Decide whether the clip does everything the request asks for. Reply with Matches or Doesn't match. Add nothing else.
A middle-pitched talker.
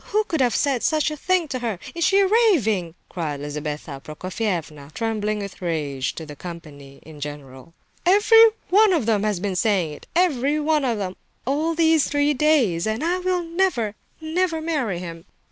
Doesn't match